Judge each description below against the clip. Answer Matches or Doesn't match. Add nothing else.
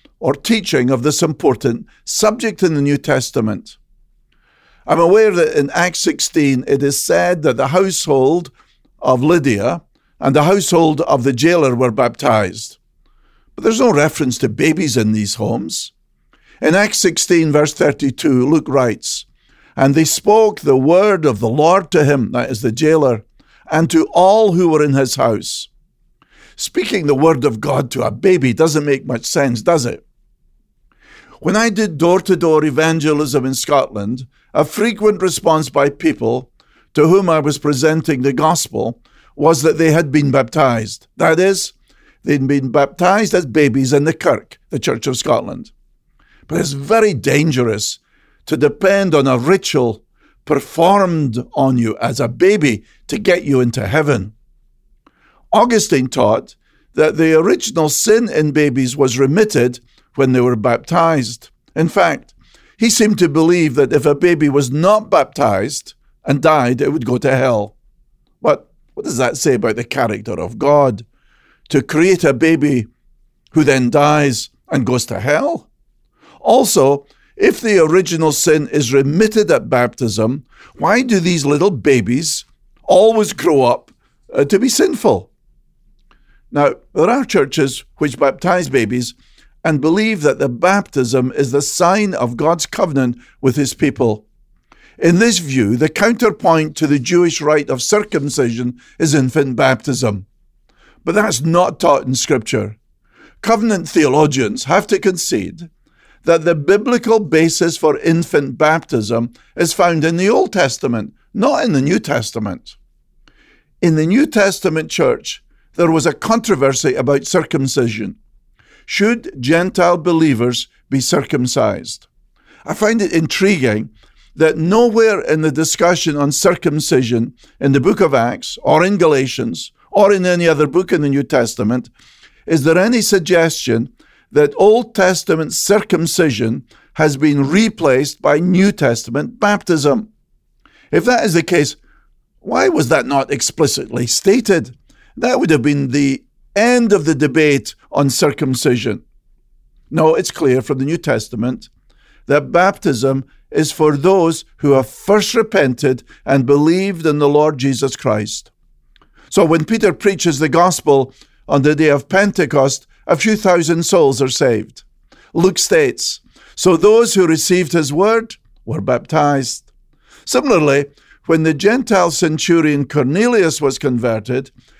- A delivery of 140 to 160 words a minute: Matches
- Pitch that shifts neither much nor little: Matches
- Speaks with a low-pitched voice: Doesn't match